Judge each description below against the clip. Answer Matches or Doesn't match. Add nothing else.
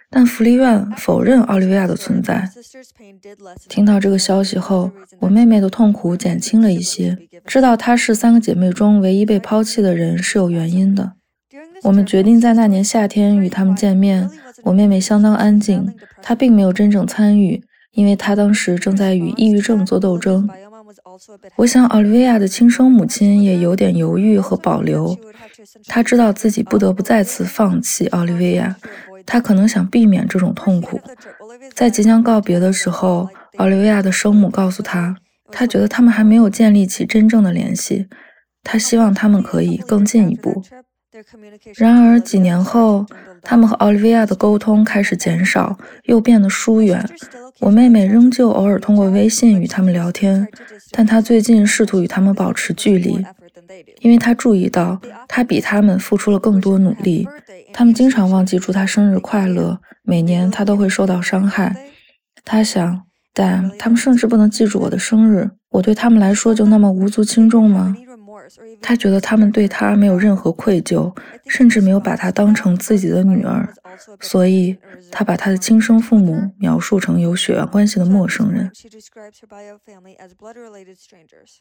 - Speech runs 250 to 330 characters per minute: Matches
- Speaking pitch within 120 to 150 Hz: Doesn't match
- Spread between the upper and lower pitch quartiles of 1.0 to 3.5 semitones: Matches